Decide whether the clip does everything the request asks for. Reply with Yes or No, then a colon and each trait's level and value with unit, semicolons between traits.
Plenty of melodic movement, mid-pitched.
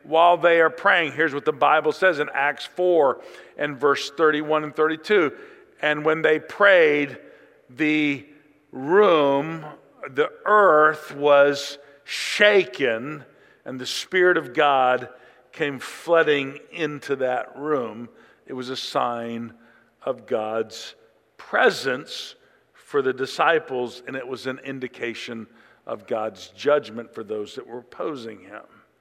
No: average, 3.6 semitones; medium, 145 Hz